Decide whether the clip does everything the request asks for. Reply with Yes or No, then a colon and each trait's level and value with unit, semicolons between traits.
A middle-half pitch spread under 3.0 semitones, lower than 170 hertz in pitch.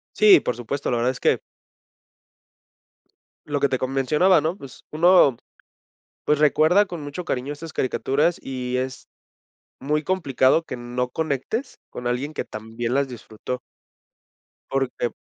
No: average, 3.8 semitones; low, 135 Hz